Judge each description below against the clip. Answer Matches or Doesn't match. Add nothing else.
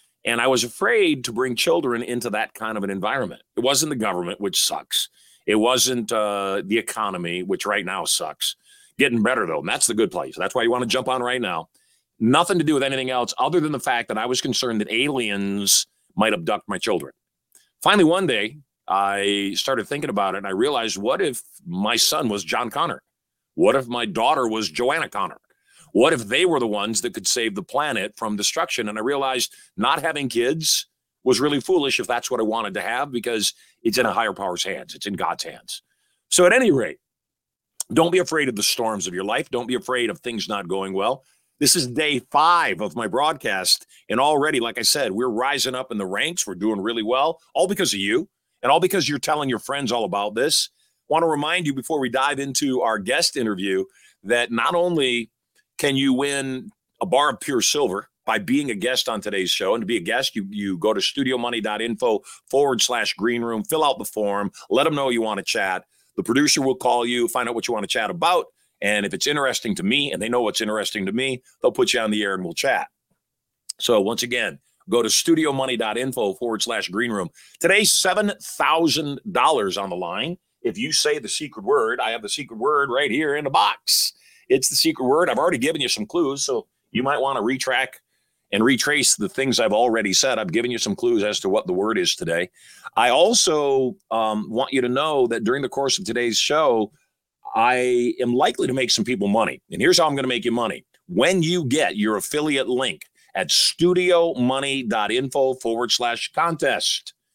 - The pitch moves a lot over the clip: Matches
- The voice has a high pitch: Doesn't match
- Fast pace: Matches